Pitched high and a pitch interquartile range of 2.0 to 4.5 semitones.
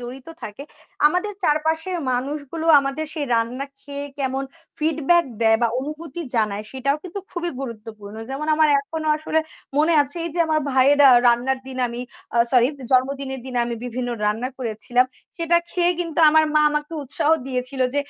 Yes: very high, 275 Hz; average, 3.9 semitones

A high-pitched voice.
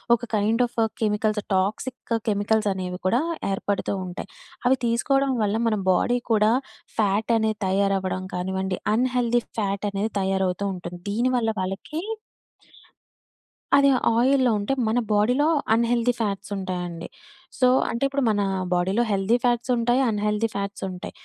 Yes: high, 210 Hz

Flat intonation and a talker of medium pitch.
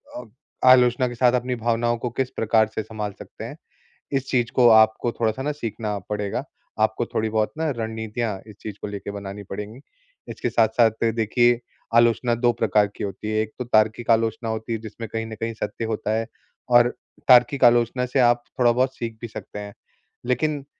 No: narrow, 1.9 semitones; low, 115 Hz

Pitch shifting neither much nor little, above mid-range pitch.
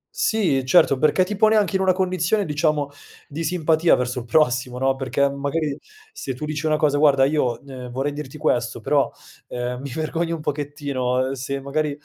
No: average, 3.3 semitones; medium, 145 Hz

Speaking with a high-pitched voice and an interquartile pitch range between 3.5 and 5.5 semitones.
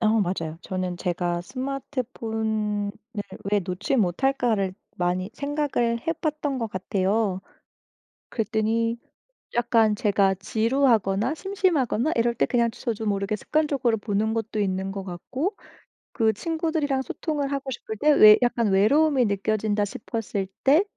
Yes: high, 225 Hz; average, 5.2 semitones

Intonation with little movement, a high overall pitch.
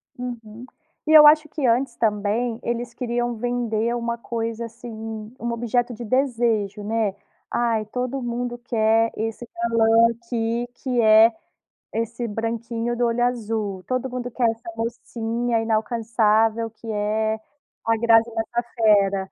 Yes: narrow, 1.4 semitones; high, 230 Hz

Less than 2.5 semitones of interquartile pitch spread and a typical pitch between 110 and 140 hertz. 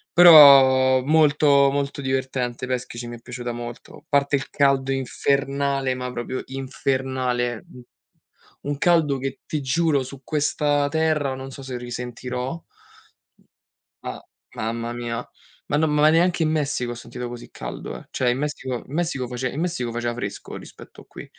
No: average, 2.8 semitones; low, 135 Hz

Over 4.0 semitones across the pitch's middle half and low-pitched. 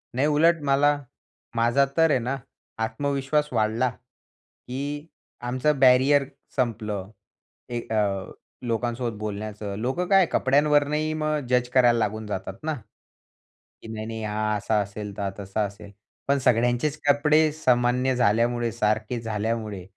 Yes: average, 4.7 semitones; low, 120 Hz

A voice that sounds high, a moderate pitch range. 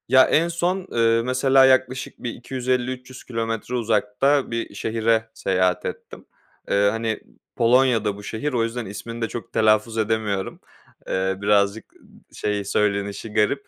No: low, 115 Hz; average, 3.4 semitones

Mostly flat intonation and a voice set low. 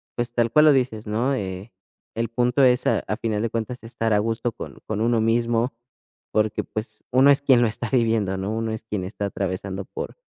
Yes: narrow, 2.3 semitones; low, 115 Hz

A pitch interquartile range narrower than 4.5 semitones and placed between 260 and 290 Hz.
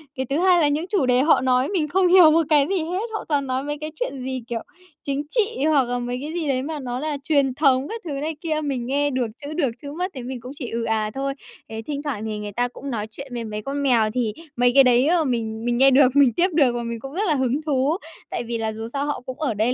Yes: average, 3.8 semitones; very high, 275 Hz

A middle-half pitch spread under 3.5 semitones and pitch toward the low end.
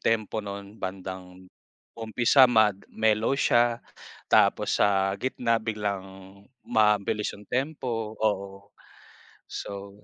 Yes: narrow, 2.5 semitones; low, 105 Hz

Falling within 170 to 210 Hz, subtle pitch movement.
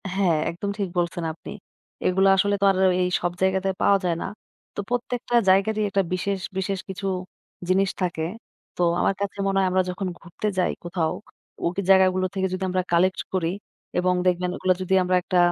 Yes: medium, 185 Hz; narrow, 1.4 semitones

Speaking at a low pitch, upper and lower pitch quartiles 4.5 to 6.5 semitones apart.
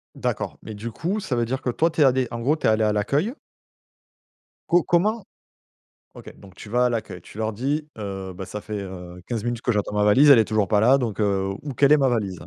Yes: low, 115 Hz; average, 5.0 semitones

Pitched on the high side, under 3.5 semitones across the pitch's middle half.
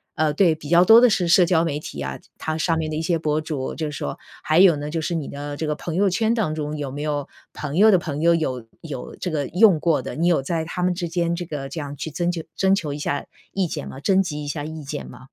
No: medium, 160 Hz; average, 3.0 semitones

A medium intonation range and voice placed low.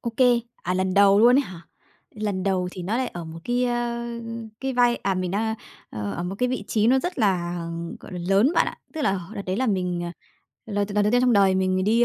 No: average, 4.4 semitones; high, 205 Hz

